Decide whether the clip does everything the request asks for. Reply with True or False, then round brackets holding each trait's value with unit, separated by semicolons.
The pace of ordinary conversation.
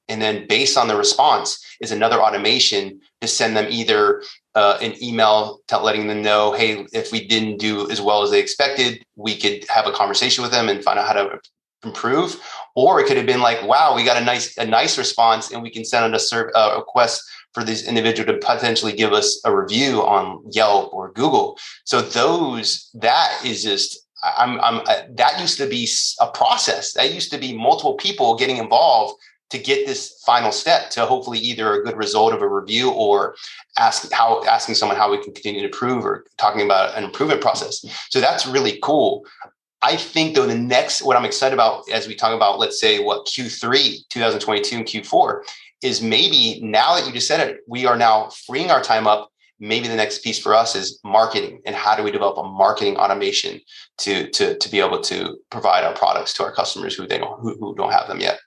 False (215 wpm)